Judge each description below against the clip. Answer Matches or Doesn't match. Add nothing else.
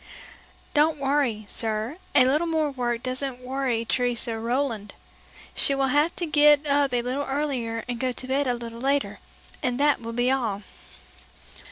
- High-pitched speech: Matches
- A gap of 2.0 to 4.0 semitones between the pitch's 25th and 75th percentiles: Matches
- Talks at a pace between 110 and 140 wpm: Doesn't match